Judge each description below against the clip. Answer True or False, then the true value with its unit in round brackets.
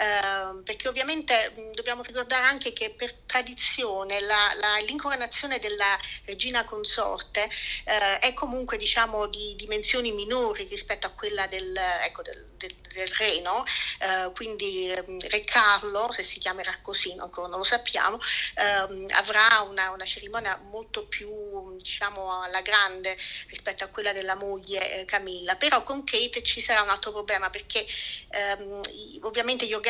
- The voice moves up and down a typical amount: True (3.6 semitones)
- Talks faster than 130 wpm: True (145 wpm)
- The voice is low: False (210 Hz)